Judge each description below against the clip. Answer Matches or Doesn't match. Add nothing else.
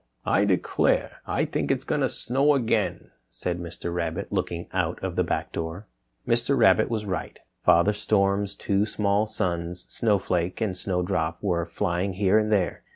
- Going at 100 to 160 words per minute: Doesn't match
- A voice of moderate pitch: Doesn't match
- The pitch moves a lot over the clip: Doesn't match